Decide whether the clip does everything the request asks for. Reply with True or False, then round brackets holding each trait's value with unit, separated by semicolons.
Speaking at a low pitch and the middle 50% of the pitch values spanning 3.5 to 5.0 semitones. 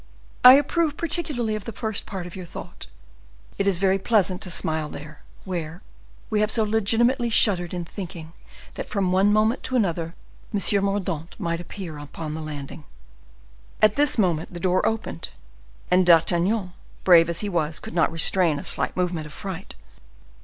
False (185 Hz; 4.2 semitones)